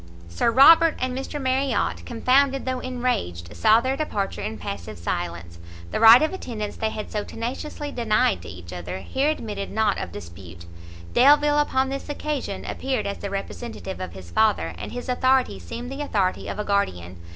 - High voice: Yes, high, 220 Hz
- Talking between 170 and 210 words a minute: Yes, average, 175 wpm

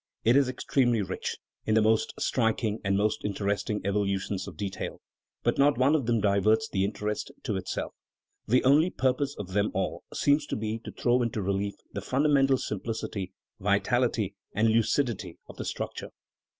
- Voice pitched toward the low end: Yes, low, 110 Hz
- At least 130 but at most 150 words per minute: No, average, 170 wpm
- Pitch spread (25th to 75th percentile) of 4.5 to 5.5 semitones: No, average, 4.0 semitones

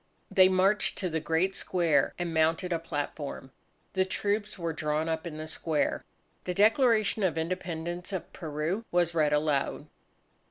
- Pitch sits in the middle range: Yes, medium, 170 Hz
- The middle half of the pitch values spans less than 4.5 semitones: Yes, average, 3.0 semitones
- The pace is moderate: Yes, average, 155 wpm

